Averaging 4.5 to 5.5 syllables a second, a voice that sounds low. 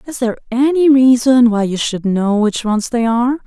No: 5.1 syllables/s; high, 240 Hz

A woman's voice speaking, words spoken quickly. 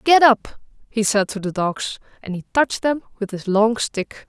Yes: female; fast, 210 wpm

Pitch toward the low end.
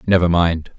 Yes: very low, 85 Hz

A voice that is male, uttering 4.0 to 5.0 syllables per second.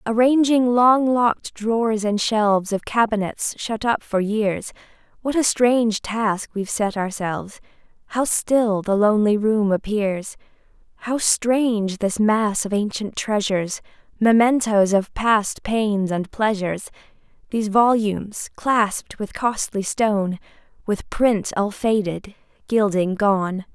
No: female; 4.1 syllables/s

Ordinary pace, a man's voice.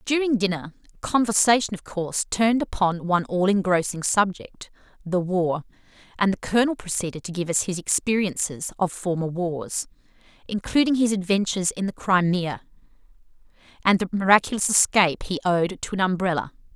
No: average, 145 wpm; female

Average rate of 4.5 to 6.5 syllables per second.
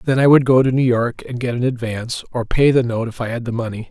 Yes: 6.3 syllables/s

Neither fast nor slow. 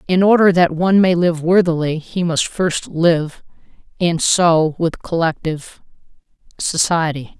No: slow, 130 wpm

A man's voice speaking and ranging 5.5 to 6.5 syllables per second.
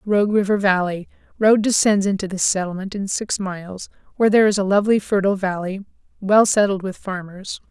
No: female; 5.9 syllables/s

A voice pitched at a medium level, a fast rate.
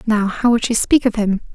No: high, 220 Hz; fast, 270 wpm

